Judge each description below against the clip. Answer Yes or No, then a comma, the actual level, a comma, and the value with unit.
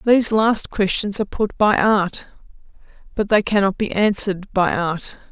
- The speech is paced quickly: No, average, 160 wpm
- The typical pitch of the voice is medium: No, high, 200 Hz